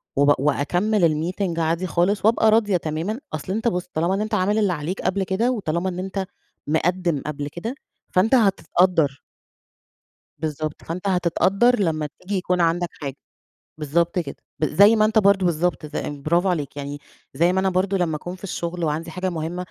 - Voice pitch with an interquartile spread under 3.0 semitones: No, average, 3.6 semitones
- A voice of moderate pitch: Yes, medium, 180 Hz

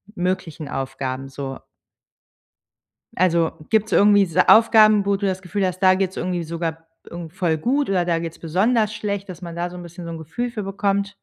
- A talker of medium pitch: Yes, medium, 180 Hz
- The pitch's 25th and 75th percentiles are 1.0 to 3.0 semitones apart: No, average, 3.4 semitones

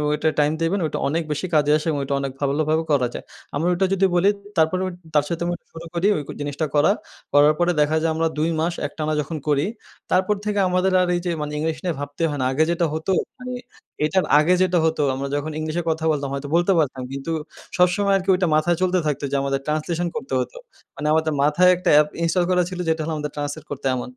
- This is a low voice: No, medium, 160 Hz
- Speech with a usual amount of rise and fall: Yes, average, 3.1 semitones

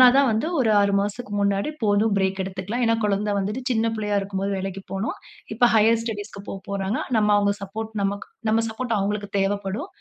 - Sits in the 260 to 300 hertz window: No, high, 205 Hz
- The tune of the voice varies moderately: No, narrow, 2.1 semitones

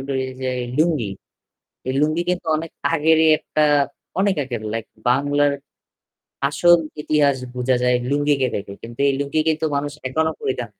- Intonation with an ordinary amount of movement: Yes, average, 3.5 semitones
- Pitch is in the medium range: Yes, medium, 145 Hz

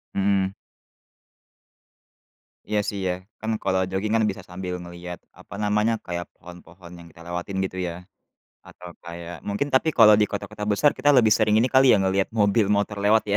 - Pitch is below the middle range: Yes, low, 100 Hz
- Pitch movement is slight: No, average, 3.2 semitones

